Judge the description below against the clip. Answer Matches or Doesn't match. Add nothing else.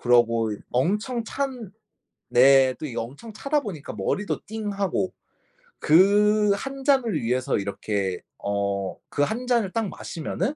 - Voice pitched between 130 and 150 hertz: Doesn't match